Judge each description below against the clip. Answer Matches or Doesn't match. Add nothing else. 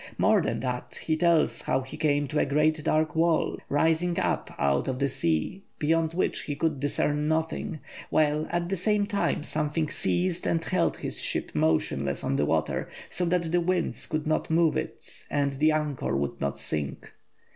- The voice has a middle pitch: Matches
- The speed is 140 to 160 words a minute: Doesn't match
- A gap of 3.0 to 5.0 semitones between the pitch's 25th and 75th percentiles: Matches